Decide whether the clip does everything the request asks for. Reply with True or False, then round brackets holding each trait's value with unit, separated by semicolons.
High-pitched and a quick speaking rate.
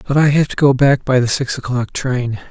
False (130 Hz; 265 wpm)